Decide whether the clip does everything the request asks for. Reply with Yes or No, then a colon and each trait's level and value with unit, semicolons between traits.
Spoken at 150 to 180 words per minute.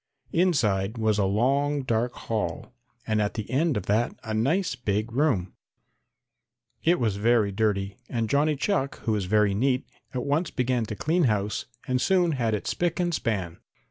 Yes: average, 175 wpm